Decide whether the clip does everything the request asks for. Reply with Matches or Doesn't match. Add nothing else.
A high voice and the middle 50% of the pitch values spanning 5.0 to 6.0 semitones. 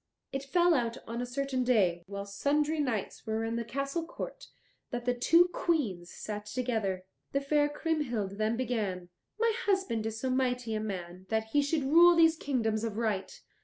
Matches